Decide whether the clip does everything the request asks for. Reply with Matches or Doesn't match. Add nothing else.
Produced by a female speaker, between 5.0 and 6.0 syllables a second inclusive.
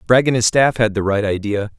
Doesn't match